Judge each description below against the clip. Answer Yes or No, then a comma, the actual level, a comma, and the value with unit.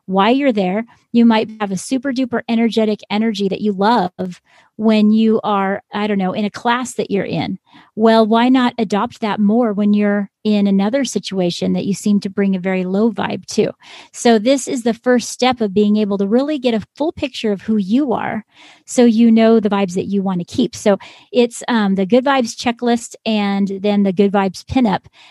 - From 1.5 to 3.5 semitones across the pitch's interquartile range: Yes, average, 3.0 semitones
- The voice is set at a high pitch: Yes, high, 215 Hz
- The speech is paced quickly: Yes, fast, 210 wpm